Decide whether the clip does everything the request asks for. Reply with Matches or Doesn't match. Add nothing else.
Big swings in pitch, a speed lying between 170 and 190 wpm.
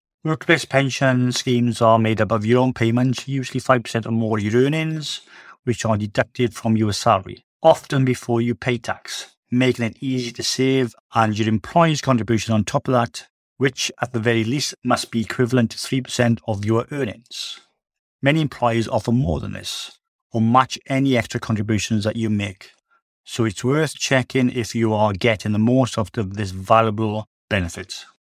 Doesn't match